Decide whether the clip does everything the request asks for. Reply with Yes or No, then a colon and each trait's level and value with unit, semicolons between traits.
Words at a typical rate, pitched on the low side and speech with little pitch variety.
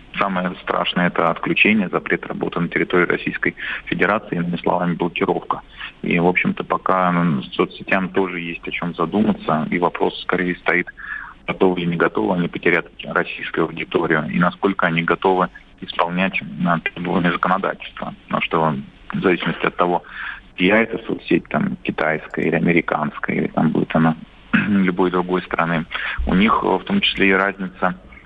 Yes: average, 145 wpm; very low, 90 Hz; narrow, 1.9 semitones